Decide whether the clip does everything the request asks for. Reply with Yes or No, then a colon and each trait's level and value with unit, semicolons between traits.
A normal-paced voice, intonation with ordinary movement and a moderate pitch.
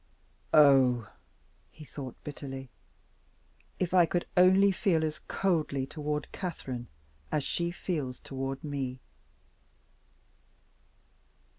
No: slow, 95 wpm; average, 4.5 semitones; medium, 150 Hz